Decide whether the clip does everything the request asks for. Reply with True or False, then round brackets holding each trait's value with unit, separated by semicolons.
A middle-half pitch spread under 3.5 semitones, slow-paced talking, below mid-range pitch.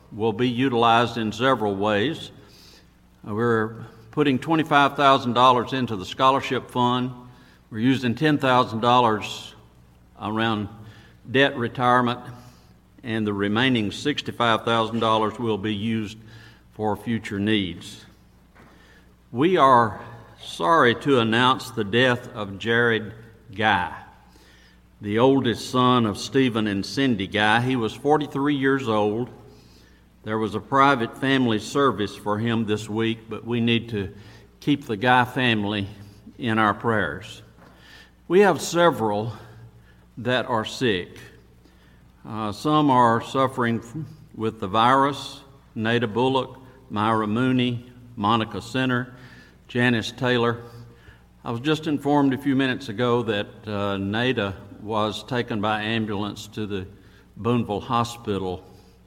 True (3.1 semitones; 115 wpm; 115 Hz)